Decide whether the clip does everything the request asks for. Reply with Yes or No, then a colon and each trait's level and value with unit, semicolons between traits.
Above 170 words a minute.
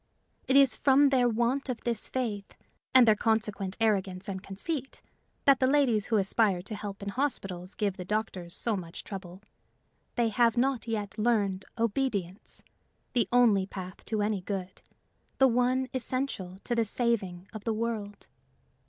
No: average, 160 wpm